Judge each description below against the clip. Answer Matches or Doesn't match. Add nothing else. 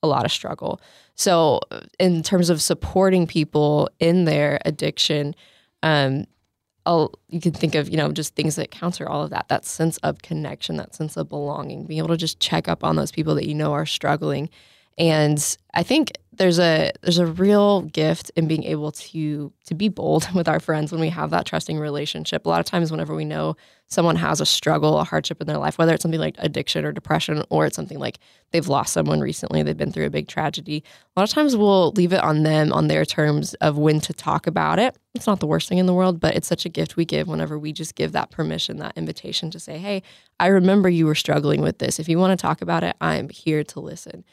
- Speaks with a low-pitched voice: Doesn't match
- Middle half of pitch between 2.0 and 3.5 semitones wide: Matches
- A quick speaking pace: Matches